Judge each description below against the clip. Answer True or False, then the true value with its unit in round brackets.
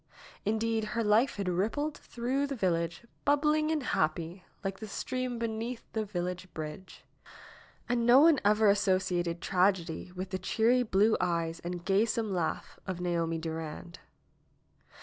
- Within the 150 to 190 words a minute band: False (140 wpm)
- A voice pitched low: False (200 Hz)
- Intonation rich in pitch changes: False (4.8 semitones)